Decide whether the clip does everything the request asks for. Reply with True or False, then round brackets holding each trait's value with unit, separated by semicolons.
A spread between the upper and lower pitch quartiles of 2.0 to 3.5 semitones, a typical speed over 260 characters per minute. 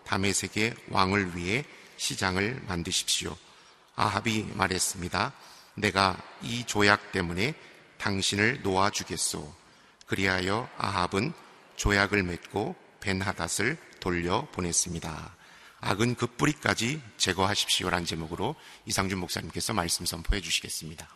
True (2.7 semitones; 285 characters per minute)